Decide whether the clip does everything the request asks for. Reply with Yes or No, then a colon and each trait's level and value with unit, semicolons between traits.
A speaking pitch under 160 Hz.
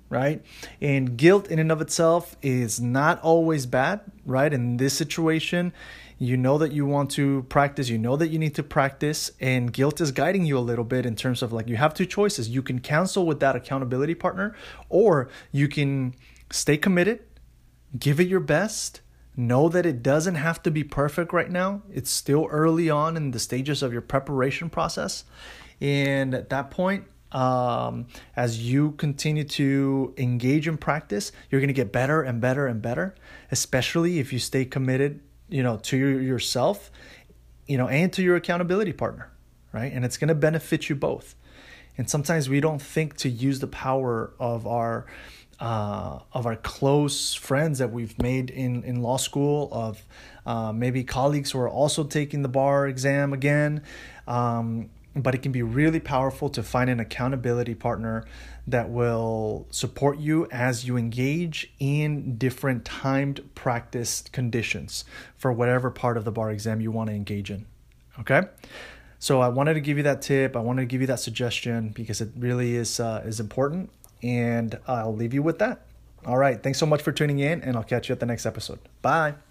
Yes: low, 135 Hz